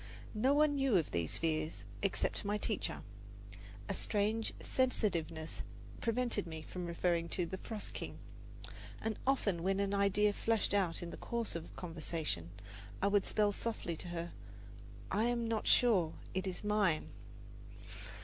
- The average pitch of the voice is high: Yes, high, 200 Hz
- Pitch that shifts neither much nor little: Yes, average, 4.6 semitones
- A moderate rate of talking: Yes, average, 150 wpm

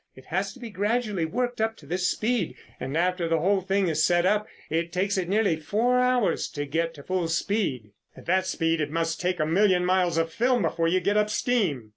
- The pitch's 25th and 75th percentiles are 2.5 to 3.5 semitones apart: No, average, 4.2 semitones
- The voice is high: No, medium, 180 Hz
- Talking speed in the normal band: No, fast, 225 wpm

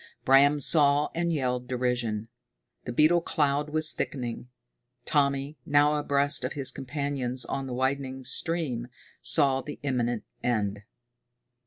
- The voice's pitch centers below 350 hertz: Yes, low, 135 Hz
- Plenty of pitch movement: No, average, 2.8 semitones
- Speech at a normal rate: No, slow, 125 wpm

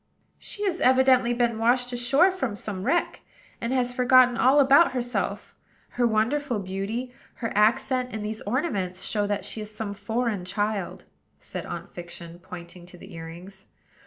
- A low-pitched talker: No, high, 225 Hz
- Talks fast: No, average, 160 wpm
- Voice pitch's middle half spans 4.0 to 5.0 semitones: Yes, average, 4.4 semitones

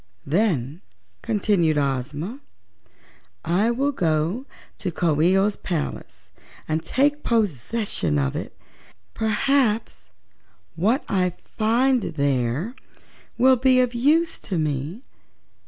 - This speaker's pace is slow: Yes, slow, 105 wpm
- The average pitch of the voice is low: No, high, 195 Hz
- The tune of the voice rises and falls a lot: Yes, wide, 7.6 semitones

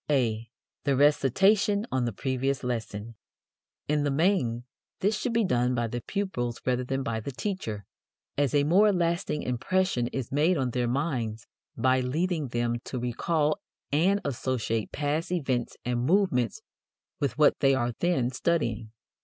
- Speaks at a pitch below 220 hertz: Yes, low, 135 Hz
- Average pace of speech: Yes, average, 155 wpm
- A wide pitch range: Yes, wide, 5.8 semitones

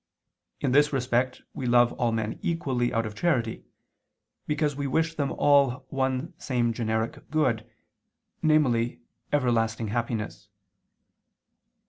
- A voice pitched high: No, low, 125 Hz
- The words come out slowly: Yes, slow, 115 wpm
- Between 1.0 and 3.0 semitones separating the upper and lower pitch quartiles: No, average, 3.6 semitones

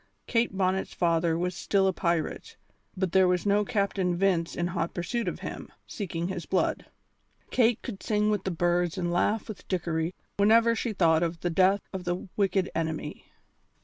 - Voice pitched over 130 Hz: Yes, medium, 185 Hz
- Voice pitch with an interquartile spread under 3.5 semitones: Yes, average, 2.7 semitones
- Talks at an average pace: Yes, average, 180 wpm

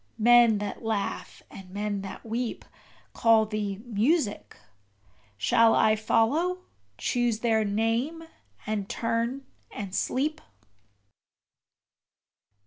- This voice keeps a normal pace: No, slow, 95 wpm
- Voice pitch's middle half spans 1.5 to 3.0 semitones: Yes, narrow, 2.5 semitones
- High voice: Yes, high, 225 Hz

